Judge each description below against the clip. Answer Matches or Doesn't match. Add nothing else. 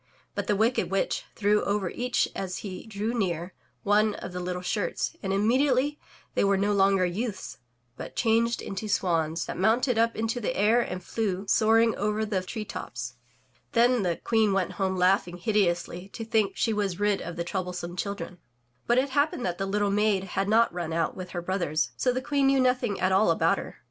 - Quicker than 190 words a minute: Matches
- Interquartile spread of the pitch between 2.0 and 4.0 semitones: Matches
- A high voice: Matches